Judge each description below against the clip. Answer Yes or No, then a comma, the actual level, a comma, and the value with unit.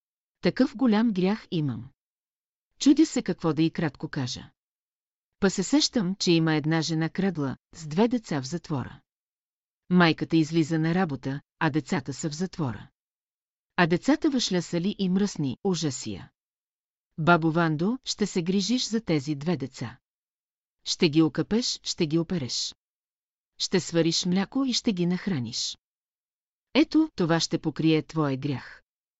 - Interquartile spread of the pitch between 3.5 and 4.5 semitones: Yes, average, 4.1 semitones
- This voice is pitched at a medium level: Yes, medium, 170 Hz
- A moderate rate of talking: Yes, average, 140 wpm